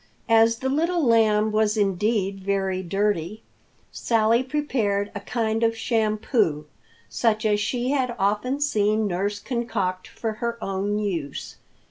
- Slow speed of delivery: Yes, slow, 130 wpm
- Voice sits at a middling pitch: No, high, 215 Hz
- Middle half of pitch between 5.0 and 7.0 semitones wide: No, average, 2.7 semitones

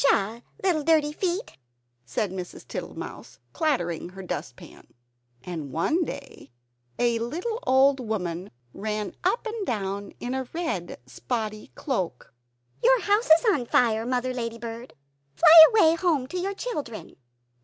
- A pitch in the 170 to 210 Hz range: No, very high, 250 Hz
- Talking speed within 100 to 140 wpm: Yes, slow, 135 wpm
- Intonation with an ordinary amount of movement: No, wide, 7.6 semitones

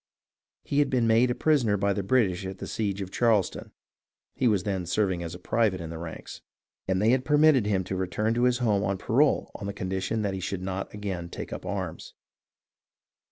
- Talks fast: Yes, fast, 210 wpm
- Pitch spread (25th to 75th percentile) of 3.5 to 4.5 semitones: Yes, average, 3.8 semitones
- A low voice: Yes, low, 100 Hz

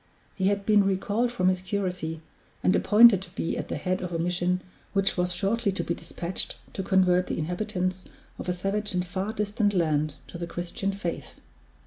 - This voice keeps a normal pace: Yes, average, 190 wpm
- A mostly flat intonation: Yes, narrow, 2.2 semitones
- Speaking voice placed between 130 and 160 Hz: No, medium, 185 Hz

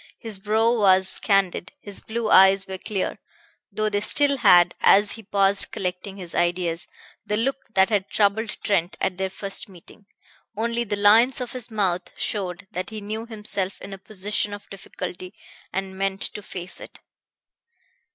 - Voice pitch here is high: Yes, high, 200 Hz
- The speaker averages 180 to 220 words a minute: No, average, 165 wpm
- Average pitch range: No, narrow, 2.3 semitones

